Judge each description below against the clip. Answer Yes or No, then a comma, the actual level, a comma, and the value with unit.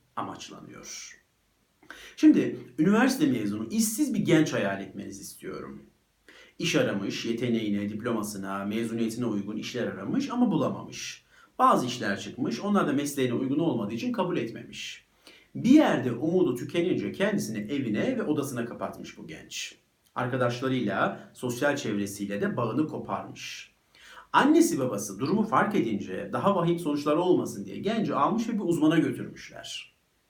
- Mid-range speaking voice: No, low, 130 Hz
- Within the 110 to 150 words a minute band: Yes, average, 125 wpm